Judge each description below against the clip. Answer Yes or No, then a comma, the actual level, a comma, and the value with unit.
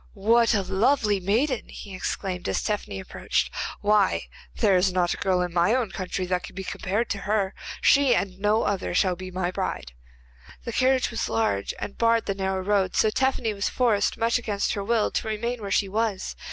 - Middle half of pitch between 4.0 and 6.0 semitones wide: No, average, 3.4 semitones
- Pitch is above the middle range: Yes, high, 205 Hz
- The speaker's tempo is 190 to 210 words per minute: Yes, average, 200 wpm